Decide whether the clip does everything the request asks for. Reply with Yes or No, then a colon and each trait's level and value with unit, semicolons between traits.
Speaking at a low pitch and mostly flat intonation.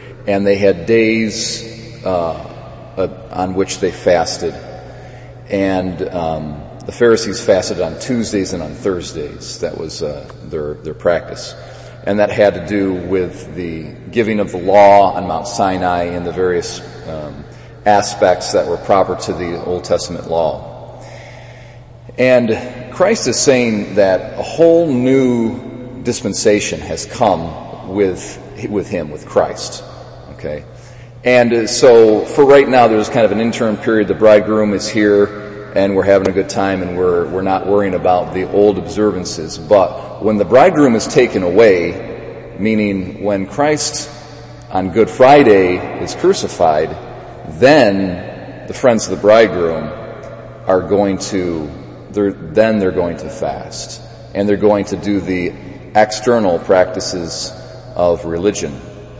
No: low, 105 Hz; average, 3.7 semitones